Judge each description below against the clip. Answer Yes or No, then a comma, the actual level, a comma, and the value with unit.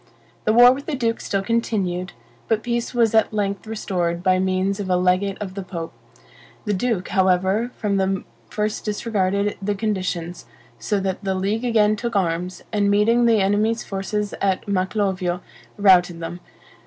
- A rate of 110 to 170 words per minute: Yes, average, 165 wpm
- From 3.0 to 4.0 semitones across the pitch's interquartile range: No, narrow, 2.6 semitones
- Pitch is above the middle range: Yes, high, 200 Hz